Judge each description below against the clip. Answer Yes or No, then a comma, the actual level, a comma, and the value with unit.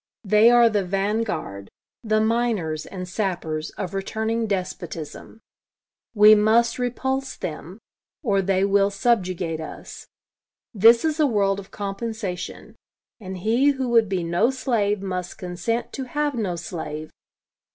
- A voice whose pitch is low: No, high, 205 Hz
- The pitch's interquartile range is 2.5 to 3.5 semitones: No, average, 4.2 semitones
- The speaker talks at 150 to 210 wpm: No, slow, 135 wpm